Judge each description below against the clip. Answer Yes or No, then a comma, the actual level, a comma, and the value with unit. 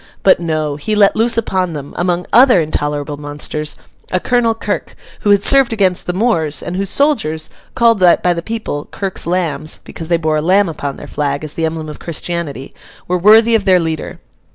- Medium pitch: Yes, medium, 175 Hz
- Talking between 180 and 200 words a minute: Yes, average, 185 wpm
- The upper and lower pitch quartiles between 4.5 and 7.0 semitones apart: Yes, average, 4.8 semitones